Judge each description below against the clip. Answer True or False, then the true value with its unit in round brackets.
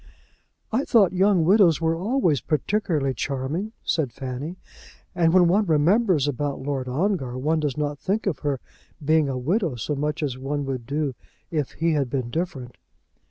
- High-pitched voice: False (150 Hz)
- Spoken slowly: False (165 wpm)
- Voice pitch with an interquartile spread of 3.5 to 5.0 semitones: True (4.7 semitones)